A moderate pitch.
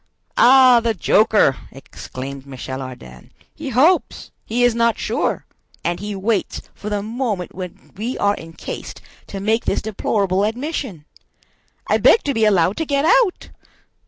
No: high, 215 Hz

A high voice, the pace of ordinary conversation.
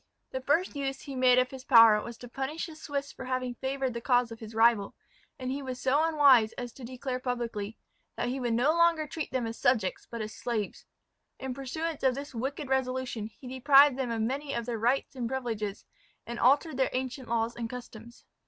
No: very high, 255 Hz; fast, 210 wpm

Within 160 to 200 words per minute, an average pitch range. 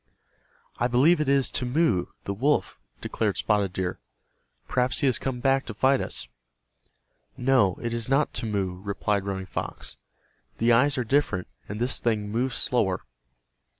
No: average, 150 wpm; average, 4.8 semitones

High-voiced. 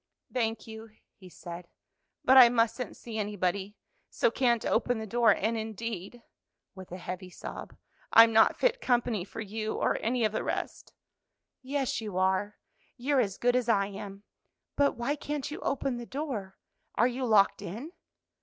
Yes: high, 225 Hz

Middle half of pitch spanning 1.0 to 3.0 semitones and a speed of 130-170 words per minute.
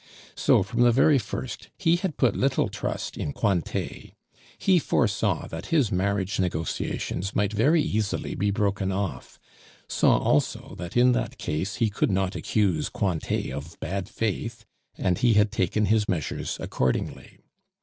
No: average, 4.3 semitones; average, 150 wpm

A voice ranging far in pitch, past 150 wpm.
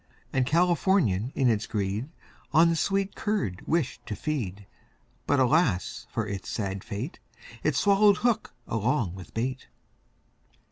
No: wide, 8.5 semitones; slow, 135 wpm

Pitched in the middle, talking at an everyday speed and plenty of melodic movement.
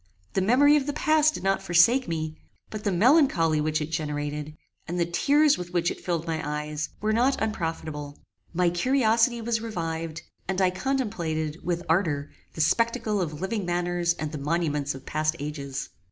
Yes: medium, 175 Hz; average, 175 wpm; wide, 6.0 semitones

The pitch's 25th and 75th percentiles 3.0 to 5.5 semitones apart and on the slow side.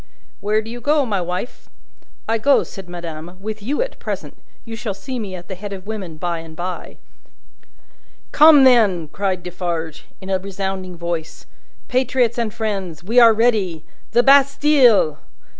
No: average, 5.0 semitones; average, 160 wpm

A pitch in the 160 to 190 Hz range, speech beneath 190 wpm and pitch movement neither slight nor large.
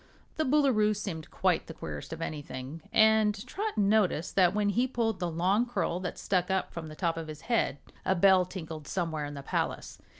No: medium, 185 Hz; average, 200 wpm; average, 4.9 semitones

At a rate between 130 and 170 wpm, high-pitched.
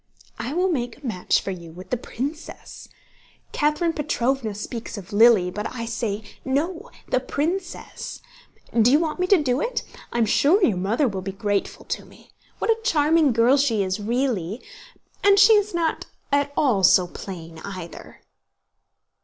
Yes: average, 165 wpm; high, 245 Hz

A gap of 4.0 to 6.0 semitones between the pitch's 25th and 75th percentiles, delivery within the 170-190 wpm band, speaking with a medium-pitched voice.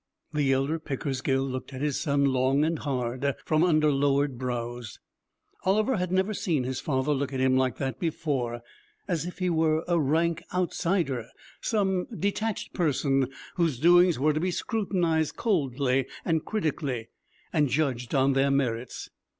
No: average, 4.3 semitones; average, 155 wpm; medium, 145 Hz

